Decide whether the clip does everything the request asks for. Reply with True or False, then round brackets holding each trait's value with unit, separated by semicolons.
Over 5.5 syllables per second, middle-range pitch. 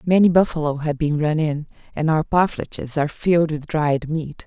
False (5.1 syllables/s; 155 Hz)